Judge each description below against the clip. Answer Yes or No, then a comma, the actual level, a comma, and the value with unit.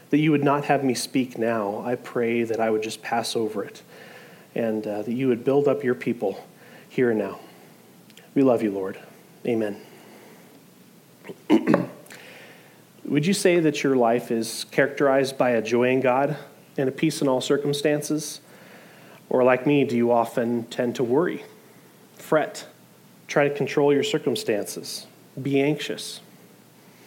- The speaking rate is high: No, average, 155 wpm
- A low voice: Yes, low, 130 Hz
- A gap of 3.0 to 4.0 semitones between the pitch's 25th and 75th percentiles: Yes, average, 3.5 semitones